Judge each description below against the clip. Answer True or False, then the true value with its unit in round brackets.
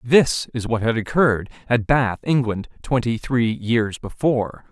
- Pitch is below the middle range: True (120 Hz)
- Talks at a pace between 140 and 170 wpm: True (155 wpm)